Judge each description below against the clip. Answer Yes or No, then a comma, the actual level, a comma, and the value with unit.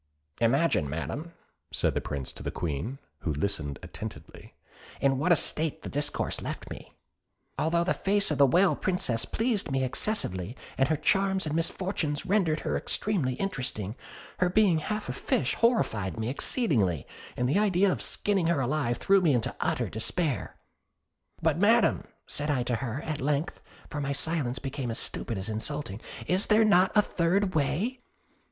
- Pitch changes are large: Yes, wide, 7.3 semitones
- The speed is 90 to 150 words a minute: No, average, 170 wpm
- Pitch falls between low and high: Yes, medium, 150 Hz